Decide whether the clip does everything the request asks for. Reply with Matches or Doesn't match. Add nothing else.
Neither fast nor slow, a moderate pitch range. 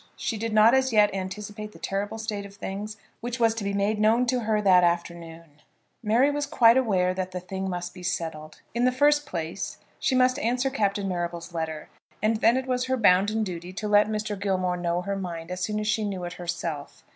Doesn't match